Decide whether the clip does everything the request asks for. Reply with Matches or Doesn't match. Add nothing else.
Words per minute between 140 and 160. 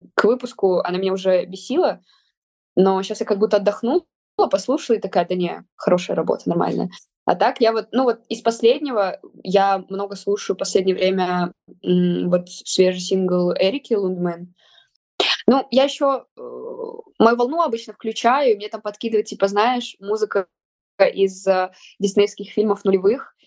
Matches